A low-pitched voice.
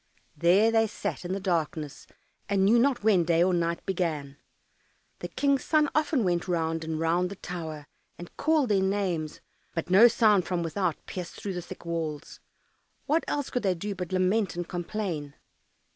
No: medium, 180 Hz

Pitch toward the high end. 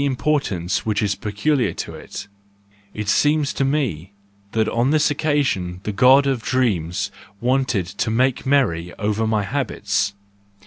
No: low, 115 Hz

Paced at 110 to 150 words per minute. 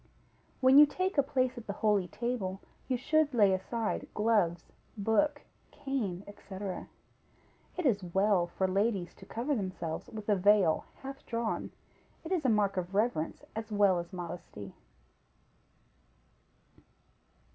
Yes: slow, 135 wpm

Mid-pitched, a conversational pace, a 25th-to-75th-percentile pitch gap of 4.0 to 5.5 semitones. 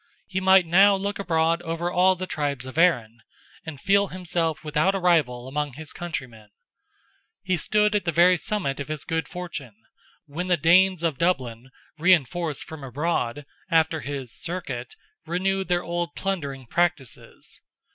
Yes: medium, 165 Hz; average, 155 wpm; average, 4.3 semitones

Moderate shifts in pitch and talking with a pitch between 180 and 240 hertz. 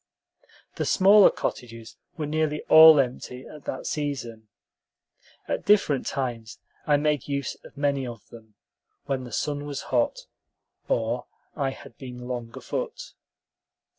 No: average, 3.7 semitones; low, 135 Hz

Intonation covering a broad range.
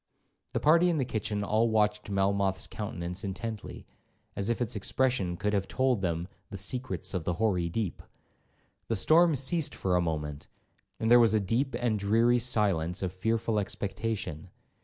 No: average, 4.0 semitones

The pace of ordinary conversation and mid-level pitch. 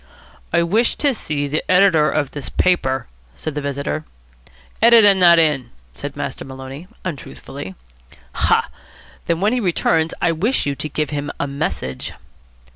Yes: average, 150 wpm; medium, 155 Hz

